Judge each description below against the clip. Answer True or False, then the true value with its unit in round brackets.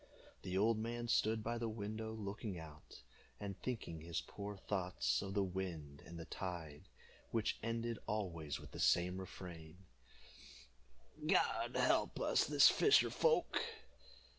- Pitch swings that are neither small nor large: True (4.4 semitones)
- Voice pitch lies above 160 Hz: False (100 Hz)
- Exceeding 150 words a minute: False (135 wpm)